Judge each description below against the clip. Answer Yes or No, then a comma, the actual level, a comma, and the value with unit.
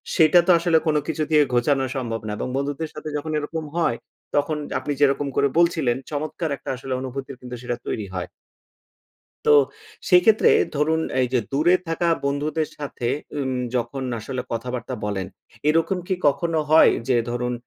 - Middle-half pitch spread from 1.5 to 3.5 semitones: No, average, 4.1 semitones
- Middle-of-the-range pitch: Yes, medium, 145 Hz